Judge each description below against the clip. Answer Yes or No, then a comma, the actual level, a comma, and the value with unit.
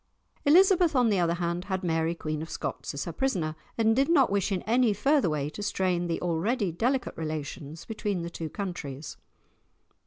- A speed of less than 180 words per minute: No, average, 185 wpm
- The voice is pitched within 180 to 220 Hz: Yes, medium, 185 Hz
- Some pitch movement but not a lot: No, wide, 6.1 semitones